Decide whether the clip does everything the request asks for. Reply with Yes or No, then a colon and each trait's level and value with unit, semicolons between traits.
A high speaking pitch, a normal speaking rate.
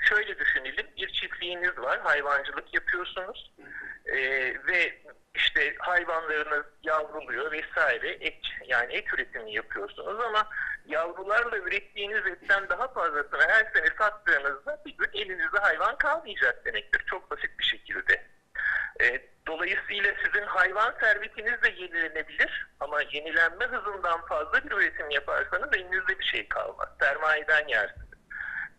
Yes: high, 210 Hz; average, 120 wpm